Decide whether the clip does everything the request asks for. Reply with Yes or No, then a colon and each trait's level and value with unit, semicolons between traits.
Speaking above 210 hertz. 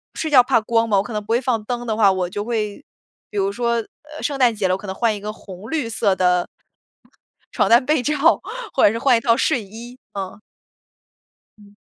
Yes: high, 225 Hz